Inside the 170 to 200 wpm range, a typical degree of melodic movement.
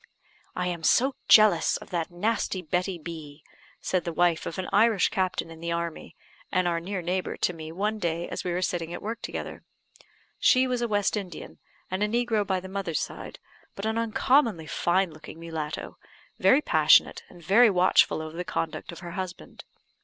Yes: average, 190 wpm; average, 3.7 semitones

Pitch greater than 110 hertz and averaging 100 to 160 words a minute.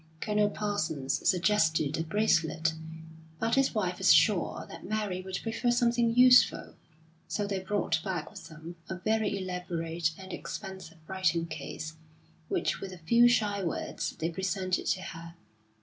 Yes: medium, 185 Hz; average, 150 wpm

